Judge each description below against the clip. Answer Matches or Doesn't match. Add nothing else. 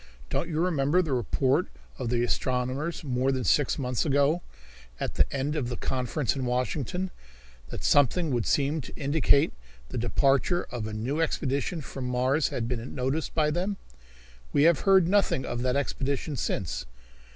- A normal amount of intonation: Matches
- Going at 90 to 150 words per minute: Doesn't match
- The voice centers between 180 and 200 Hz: Doesn't match